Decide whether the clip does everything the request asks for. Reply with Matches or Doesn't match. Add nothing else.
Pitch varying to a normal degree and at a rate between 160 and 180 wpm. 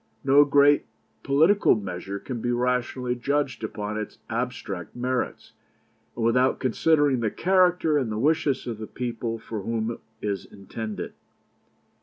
Doesn't match